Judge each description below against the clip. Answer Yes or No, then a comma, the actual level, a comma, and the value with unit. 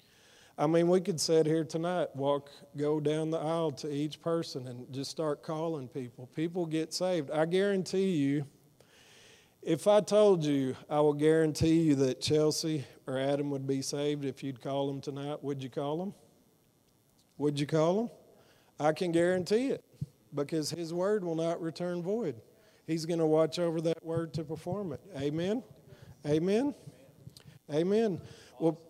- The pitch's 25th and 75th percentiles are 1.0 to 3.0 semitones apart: Yes, average, 2.7 semitones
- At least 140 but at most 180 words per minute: Yes, average, 165 wpm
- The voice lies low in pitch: No, medium, 155 Hz